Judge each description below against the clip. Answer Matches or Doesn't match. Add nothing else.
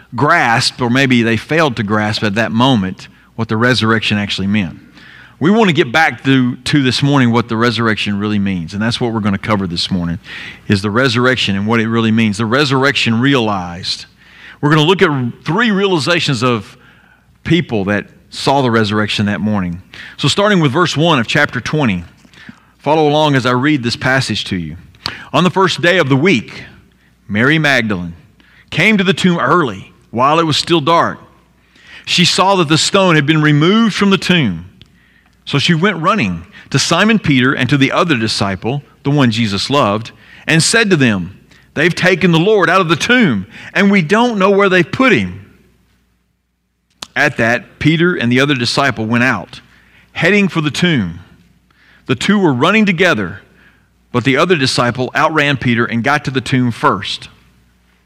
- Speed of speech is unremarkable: Matches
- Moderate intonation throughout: Doesn't match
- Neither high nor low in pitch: Doesn't match